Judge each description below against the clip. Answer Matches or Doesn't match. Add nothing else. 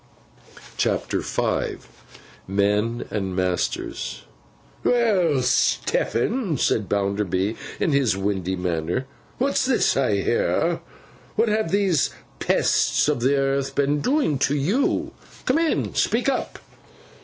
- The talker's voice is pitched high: Doesn't match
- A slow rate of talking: Matches